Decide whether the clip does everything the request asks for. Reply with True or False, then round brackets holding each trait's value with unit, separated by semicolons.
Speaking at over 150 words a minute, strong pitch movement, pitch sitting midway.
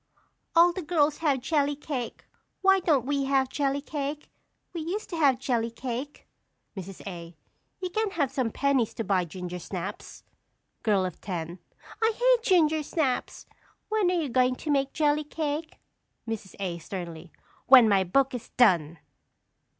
False (160 wpm; 7.0 semitones; 275 Hz)